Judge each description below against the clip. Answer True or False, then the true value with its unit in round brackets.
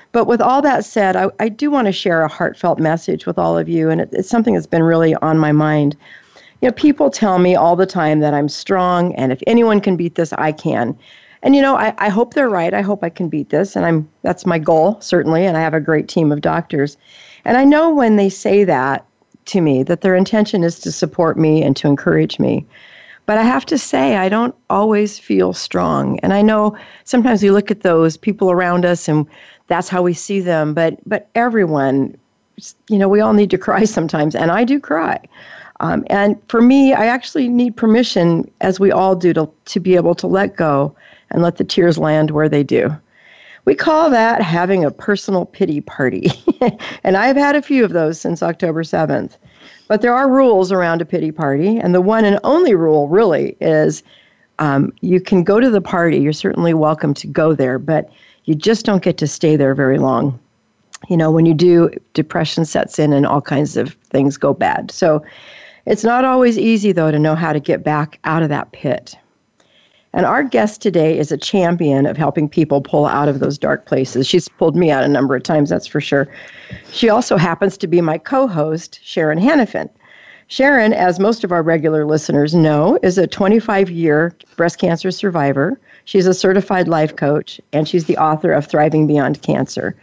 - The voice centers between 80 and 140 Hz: False (175 Hz)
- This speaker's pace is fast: True (210 wpm)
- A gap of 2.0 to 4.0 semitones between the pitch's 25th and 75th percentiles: False (5.2 semitones)